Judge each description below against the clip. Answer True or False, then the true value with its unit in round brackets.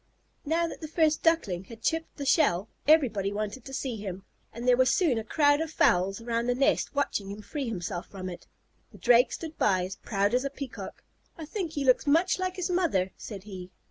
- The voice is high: True (250 Hz)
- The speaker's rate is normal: False (215 wpm)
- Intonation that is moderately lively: False (7.5 semitones)